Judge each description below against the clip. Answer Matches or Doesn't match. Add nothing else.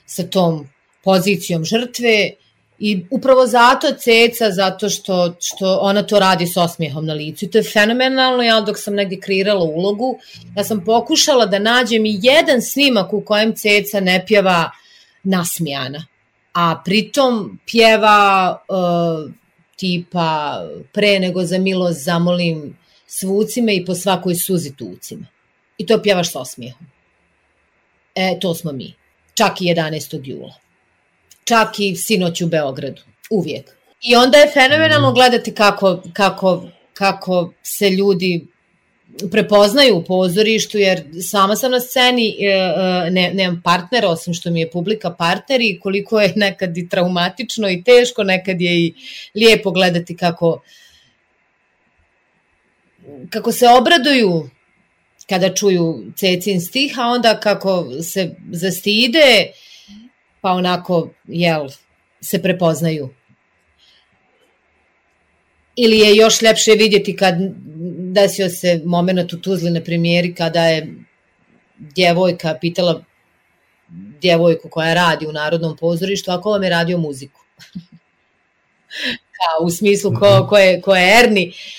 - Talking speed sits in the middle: Doesn't match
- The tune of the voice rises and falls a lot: Doesn't match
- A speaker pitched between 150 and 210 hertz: Matches